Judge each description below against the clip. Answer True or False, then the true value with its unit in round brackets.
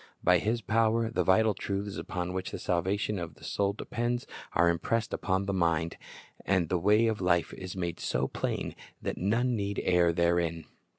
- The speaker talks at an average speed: True (180 wpm)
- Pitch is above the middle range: False (95 Hz)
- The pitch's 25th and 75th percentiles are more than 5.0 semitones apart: False (3.7 semitones)